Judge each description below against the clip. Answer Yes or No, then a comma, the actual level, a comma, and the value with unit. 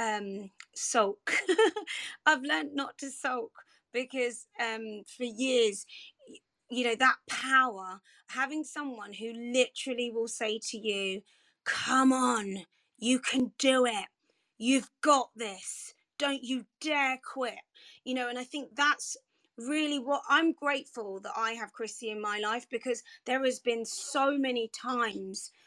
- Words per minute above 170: No, average, 140 wpm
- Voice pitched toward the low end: No, very high, 250 Hz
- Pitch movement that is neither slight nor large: Yes, average, 3.6 semitones